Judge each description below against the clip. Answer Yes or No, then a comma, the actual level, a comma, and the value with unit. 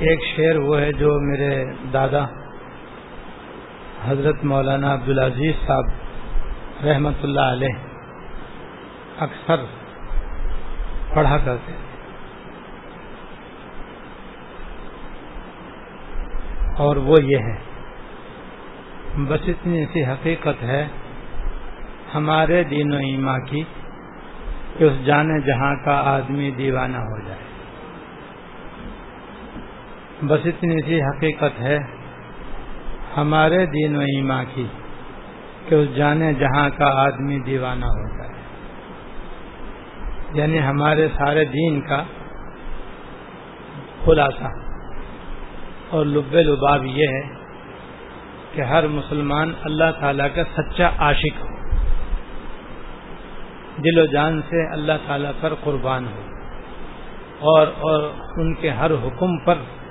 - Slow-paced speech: Yes, slow, 95 wpm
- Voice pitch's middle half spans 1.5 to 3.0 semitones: Yes, narrow, 2.5 semitones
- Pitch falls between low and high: Yes, medium, 145 Hz